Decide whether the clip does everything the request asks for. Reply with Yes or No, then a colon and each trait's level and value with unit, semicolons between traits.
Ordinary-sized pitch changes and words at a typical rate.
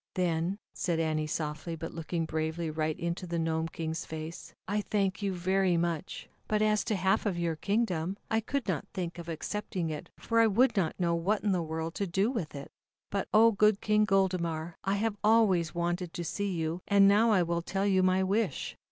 No: average, 3.6 semitones; fast, 210 wpm